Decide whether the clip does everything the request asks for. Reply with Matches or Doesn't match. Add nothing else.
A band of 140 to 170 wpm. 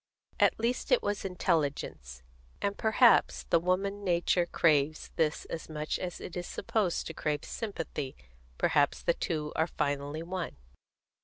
Matches